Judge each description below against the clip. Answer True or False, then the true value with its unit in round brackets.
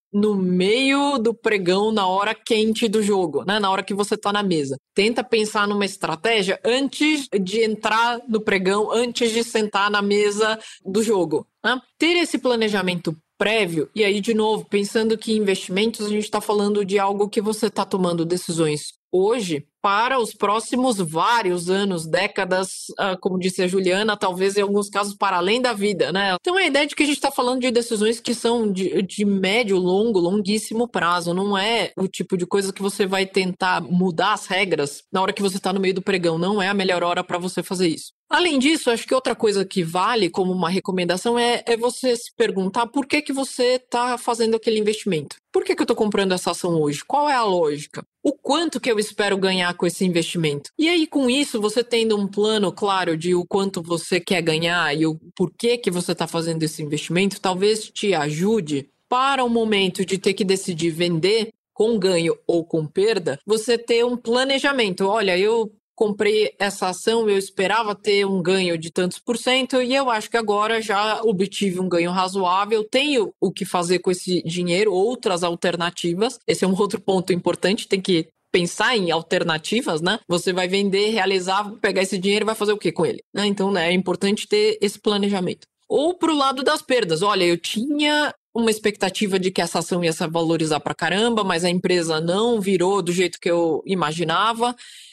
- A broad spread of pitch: False (3.7 semitones)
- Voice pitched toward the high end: True (200 Hz)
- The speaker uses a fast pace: True (195 wpm)